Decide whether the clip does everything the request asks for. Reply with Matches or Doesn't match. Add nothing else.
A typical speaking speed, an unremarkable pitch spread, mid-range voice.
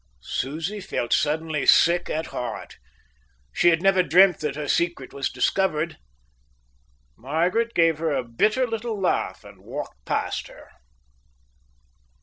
Doesn't match